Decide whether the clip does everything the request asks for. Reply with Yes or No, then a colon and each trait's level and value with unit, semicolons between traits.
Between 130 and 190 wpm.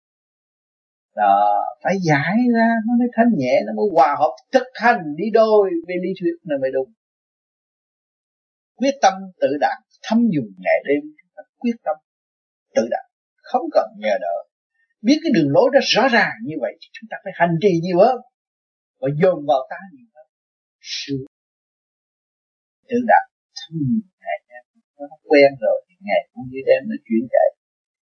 Yes: average, 170 wpm